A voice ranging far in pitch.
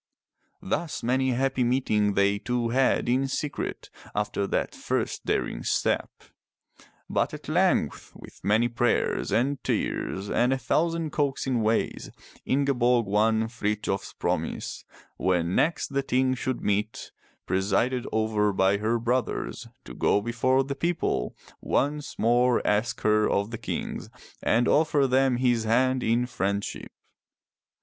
No: average, 3.7 semitones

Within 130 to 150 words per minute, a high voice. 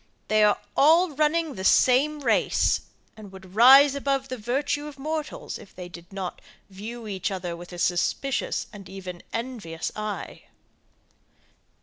Yes: average, 145 wpm; high, 225 Hz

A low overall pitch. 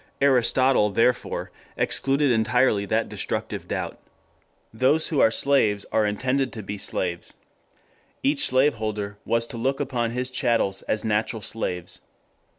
Yes: low, 115 Hz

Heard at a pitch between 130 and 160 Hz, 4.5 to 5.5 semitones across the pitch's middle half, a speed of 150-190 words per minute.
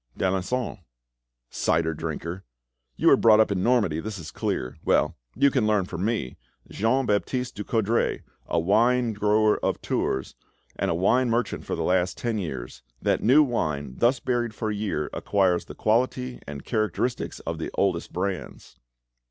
No: low, 105 Hz; average, 5.1 semitones; average, 160 wpm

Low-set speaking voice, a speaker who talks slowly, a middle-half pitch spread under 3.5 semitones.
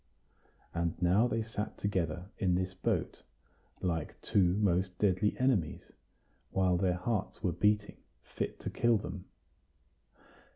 Yes: very low, 95 Hz; slow, 125 wpm; average, 2.9 semitones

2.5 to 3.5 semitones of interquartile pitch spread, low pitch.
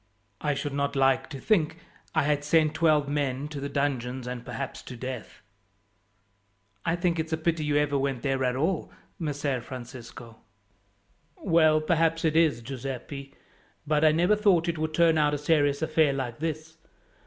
No: average, 2.9 semitones; medium, 145 Hz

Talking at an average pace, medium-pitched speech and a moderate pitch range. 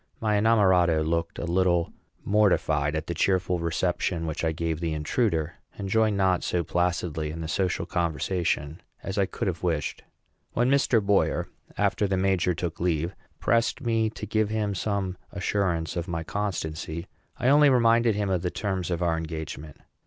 No: average, 170 wpm; very low, 90 Hz; average, 3.8 semitones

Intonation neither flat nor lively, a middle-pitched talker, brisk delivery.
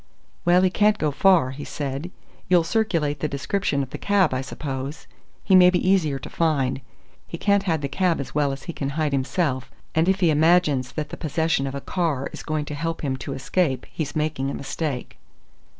Yes: average, 4.2 semitones; medium, 155 Hz; fast, 210 wpm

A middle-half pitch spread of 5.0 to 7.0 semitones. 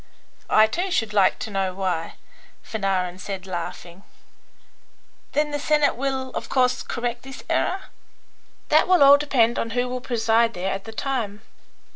Yes: wide, 5.6 semitones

